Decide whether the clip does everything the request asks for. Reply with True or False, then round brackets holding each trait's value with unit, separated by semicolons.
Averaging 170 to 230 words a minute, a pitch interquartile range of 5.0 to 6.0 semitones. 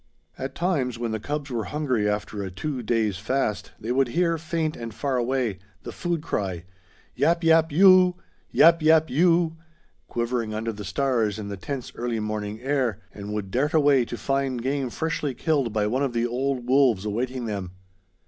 True (180 wpm; 5.4 semitones)